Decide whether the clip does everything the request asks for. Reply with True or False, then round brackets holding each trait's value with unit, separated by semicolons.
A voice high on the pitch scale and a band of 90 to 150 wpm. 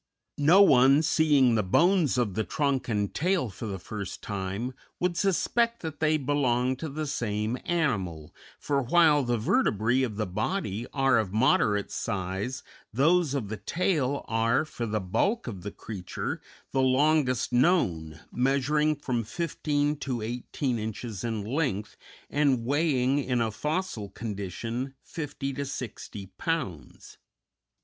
False (130 Hz; 140 wpm)